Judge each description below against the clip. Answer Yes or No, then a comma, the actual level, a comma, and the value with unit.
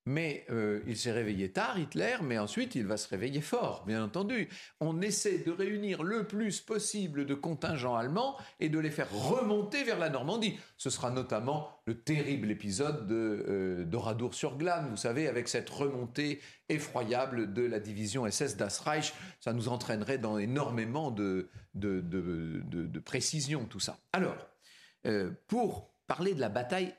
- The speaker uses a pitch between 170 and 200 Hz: No, low, 135 Hz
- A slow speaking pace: No, average, 165 wpm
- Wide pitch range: Yes, wide, 6.7 semitones